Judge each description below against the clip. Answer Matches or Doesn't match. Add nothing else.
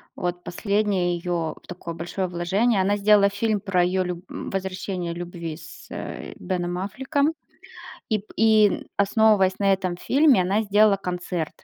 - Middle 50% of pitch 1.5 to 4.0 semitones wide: Matches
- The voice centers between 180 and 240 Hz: Matches